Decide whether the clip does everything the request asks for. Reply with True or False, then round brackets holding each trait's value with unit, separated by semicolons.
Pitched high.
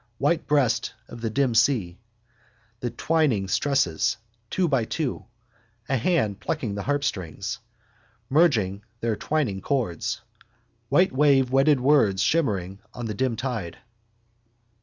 False (125 Hz)